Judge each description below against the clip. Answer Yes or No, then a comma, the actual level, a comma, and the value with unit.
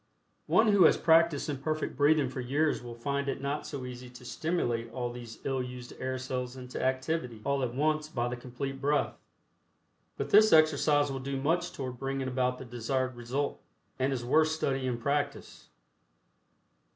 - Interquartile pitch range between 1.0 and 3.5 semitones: Yes, average, 2.7 semitones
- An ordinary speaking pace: Yes, average, 175 wpm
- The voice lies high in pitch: No, low, 135 Hz